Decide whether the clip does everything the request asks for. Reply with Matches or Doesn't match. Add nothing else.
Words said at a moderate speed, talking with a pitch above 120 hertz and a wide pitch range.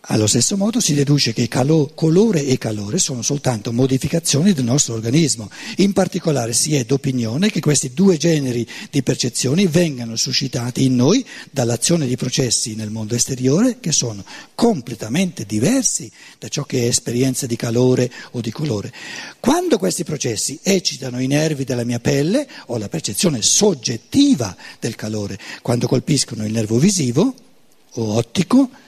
Matches